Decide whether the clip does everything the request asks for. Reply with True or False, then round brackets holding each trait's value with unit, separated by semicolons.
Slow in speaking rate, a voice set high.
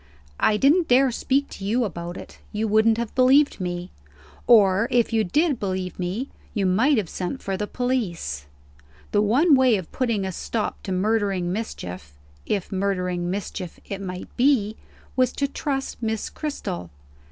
False (165 wpm; 210 Hz)